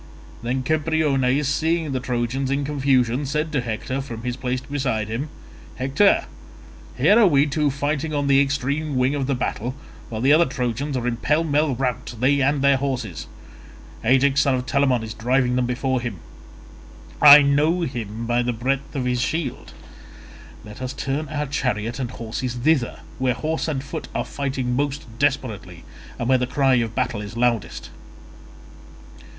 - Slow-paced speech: No, average, 170 wpm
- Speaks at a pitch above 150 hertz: No, low, 130 Hz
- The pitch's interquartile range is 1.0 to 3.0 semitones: Yes, average, 2.7 semitones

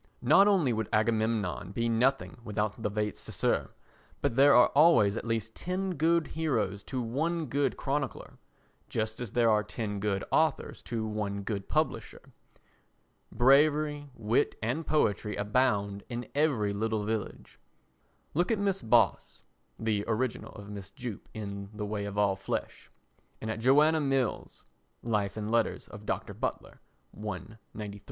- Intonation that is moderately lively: Yes, average, 4.8 semitones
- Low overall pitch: Yes, low, 115 Hz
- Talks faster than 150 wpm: No, average, 145 wpm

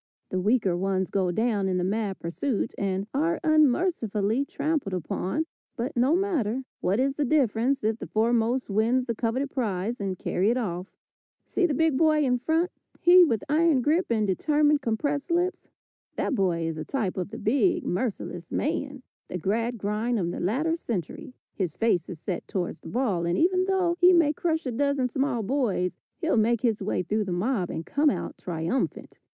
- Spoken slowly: No, average, 185 wpm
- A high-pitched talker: Yes, high, 235 Hz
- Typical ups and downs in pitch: No, wide, 6.8 semitones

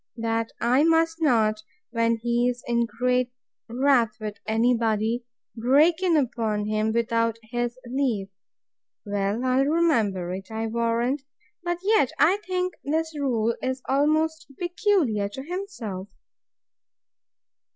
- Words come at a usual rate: No, slow, 125 wpm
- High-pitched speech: Yes, high, 240 Hz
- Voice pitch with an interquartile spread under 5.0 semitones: No, average, 5.3 semitones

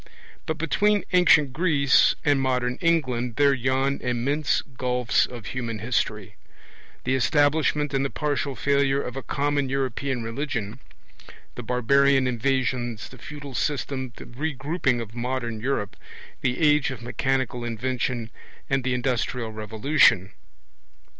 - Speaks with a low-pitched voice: Yes, low, 130 Hz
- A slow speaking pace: Yes, slow, 125 wpm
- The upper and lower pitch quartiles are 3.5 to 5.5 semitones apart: No, narrow, 2.6 semitones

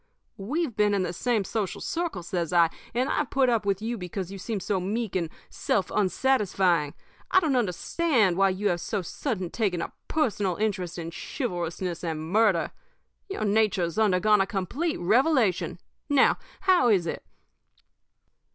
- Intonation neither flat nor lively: Yes, average, 5.0 semitones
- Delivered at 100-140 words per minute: No, average, 160 wpm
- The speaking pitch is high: Yes, high, 200 Hz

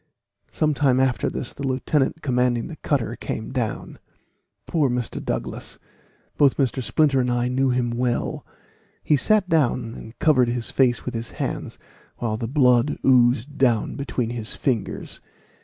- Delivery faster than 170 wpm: No, average, 155 wpm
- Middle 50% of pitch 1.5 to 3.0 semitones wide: Yes, narrow, 2.5 semitones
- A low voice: Yes, low, 125 Hz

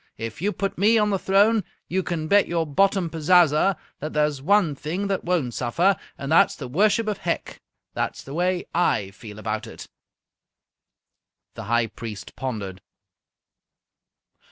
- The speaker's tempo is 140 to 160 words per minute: Yes, average, 155 wpm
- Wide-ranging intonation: Yes, wide, 7.3 semitones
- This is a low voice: No, medium, 165 Hz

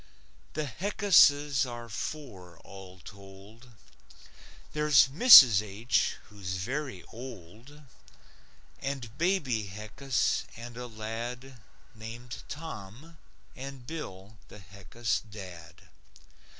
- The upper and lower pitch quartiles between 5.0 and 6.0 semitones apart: Yes, wide, 5.4 semitones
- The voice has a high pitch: No, low, 120 Hz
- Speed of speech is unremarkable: No, slow, 90 wpm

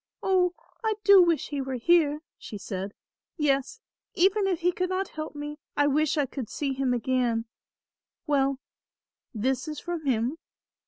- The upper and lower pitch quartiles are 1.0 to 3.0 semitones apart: No, average, 5.0 semitones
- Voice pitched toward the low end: No, very high, 295 Hz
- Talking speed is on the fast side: No, average, 160 wpm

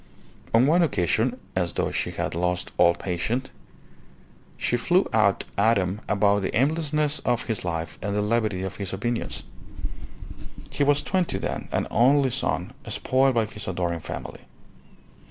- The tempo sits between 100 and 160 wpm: Yes, average, 155 wpm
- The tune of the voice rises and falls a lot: Yes, wide, 5.8 semitones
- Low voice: Yes, low, 110 Hz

